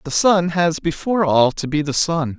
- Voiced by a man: Yes, male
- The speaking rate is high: Yes, fast, 225 wpm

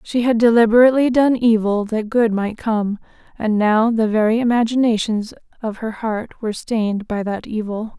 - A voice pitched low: No, high, 225 Hz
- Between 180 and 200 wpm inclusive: No, average, 165 wpm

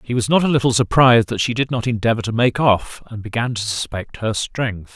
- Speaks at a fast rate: Yes, fast, 240 wpm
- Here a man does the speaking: Yes, male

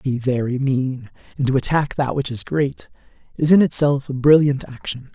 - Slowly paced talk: No, average, 200 wpm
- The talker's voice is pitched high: No, low, 135 Hz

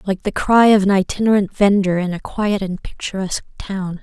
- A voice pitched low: No, high, 195 Hz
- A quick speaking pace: No, average, 195 wpm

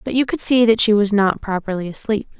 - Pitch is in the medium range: No, high, 215 Hz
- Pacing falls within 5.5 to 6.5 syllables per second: Yes, 5.9 syllables/s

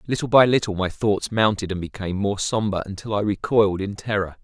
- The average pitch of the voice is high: No, low, 100 Hz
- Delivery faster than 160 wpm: Yes, fast, 205 wpm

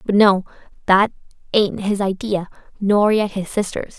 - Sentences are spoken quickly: No, average, 150 wpm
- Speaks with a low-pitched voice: No, high, 200 Hz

